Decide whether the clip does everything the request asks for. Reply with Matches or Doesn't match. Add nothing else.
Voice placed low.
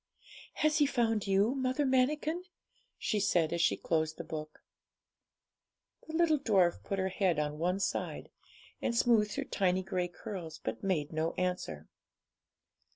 Doesn't match